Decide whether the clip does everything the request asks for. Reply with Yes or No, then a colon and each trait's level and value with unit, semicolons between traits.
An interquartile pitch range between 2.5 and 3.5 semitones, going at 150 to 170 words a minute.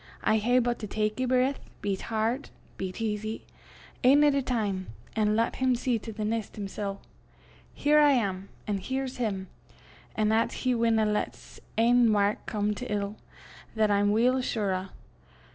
No: average, 3.2 semitones; average, 180 wpm